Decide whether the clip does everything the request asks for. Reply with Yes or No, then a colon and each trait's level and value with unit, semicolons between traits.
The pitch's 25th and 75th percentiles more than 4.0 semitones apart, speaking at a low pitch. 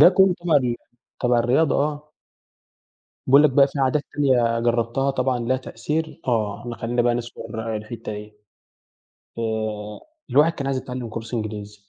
No: average, 3.5 semitones; low, 120 Hz